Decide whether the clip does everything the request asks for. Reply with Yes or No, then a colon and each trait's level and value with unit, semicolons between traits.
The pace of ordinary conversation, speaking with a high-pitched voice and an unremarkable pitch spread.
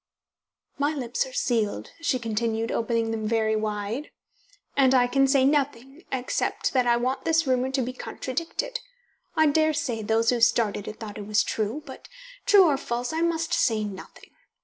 Yes: average, 170 wpm; very high, 250 Hz; average, 4.4 semitones